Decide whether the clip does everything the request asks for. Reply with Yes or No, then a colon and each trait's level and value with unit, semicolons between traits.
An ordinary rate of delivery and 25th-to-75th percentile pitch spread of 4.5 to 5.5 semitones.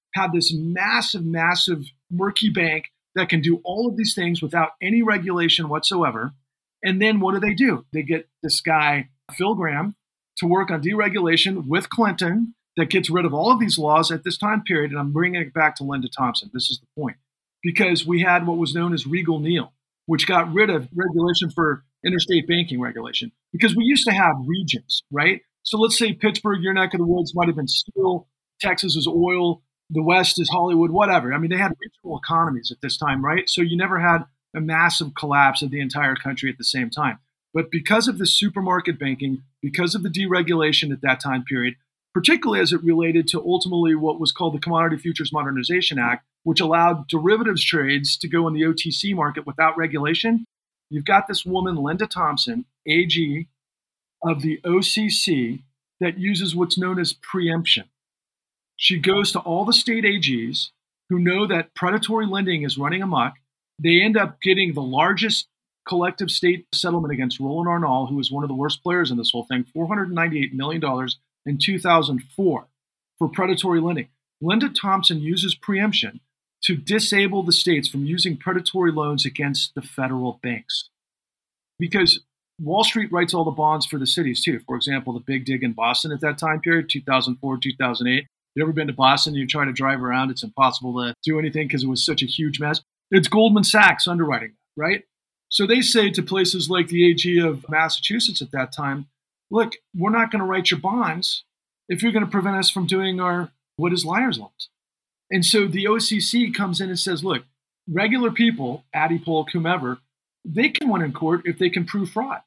Yes: average, 190 wpm; average, 4.8 semitones